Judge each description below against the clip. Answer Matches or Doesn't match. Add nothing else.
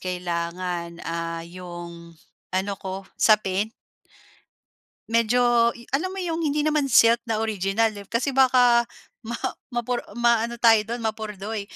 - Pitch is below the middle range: Doesn't match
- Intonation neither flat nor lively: Matches